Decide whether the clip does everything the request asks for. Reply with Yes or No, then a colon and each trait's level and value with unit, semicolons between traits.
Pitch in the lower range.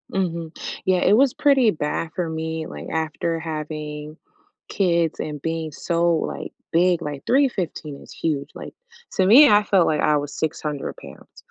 No: medium, 165 Hz